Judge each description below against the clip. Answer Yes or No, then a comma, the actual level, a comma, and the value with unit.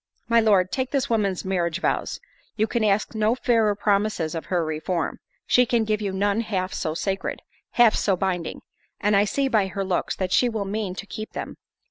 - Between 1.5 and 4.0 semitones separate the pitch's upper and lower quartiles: Yes, average, 2.9 semitones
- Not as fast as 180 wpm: No, average, 190 wpm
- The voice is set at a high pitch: Yes, high, 205 Hz